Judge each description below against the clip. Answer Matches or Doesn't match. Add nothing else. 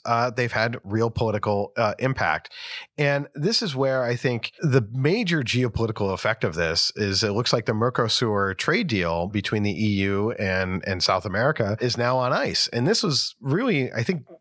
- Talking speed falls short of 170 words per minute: Doesn't match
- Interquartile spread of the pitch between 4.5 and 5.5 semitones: Doesn't match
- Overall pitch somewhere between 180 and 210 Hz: Doesn't match